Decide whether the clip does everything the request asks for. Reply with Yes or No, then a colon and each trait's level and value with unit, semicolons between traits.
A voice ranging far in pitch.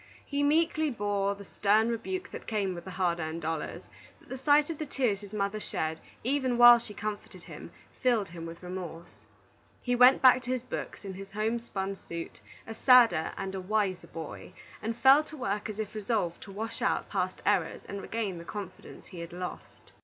No: average, 4.8 semitones